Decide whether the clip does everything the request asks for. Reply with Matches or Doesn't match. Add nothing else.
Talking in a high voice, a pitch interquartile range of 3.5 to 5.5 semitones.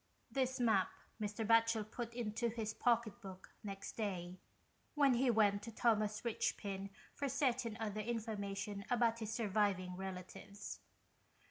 Doesn't match